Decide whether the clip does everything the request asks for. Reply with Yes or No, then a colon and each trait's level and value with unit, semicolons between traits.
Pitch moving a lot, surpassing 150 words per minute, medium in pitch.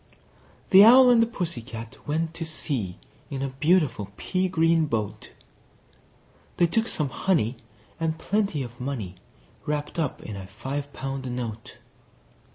No: wide, 6.0 semitones; average, 145 wpm; medium, 145 Hz